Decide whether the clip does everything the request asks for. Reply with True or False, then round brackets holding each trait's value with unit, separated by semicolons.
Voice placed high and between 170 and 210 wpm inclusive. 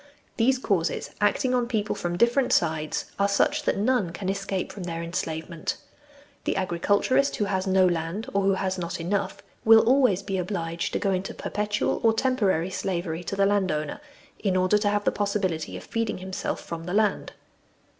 True (195 Hz; 180 wpm)